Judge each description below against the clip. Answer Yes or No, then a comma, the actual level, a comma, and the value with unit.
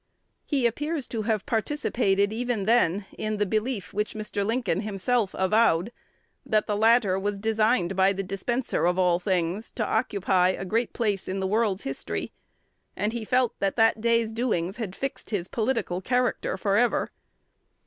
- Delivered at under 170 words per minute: Yes, average, 160 wpm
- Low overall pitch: No, high, 215 Hz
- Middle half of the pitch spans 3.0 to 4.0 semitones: Yes, average, 3.4 semitones